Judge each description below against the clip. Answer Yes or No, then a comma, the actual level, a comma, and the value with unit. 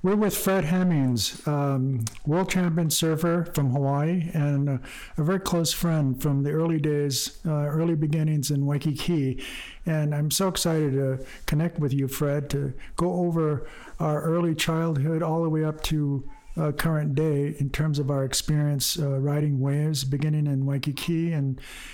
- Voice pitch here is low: No, medium, 150 Hz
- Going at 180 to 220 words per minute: No, average, 160 wpm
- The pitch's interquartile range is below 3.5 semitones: Yes, average, 2.7 semitones